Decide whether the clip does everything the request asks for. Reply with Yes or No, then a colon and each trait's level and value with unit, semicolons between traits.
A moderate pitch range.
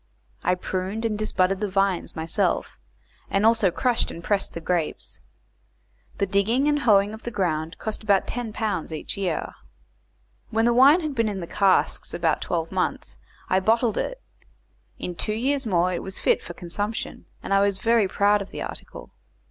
Yes: average, 3.6 semitones